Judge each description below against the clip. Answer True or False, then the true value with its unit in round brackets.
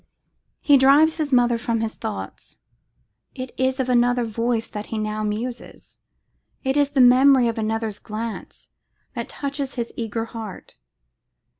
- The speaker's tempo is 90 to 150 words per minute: True (145 wpm)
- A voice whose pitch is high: True (240 Hz)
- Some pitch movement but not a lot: True (3.0 semitones)